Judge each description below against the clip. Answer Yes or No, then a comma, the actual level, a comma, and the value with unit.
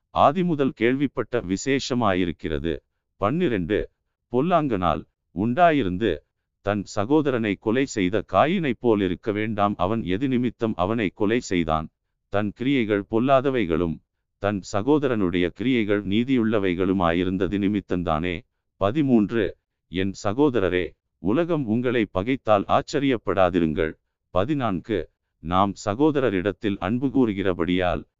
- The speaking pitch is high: No, low, 100 Hz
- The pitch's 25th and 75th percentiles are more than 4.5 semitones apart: Yes, average, 4.9 semitones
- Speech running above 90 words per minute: No, average, 85 wpm